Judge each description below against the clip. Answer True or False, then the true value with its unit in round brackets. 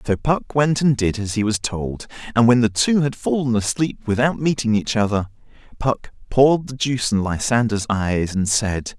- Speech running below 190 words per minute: False (195 wpm)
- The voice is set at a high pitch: False (115 Hz)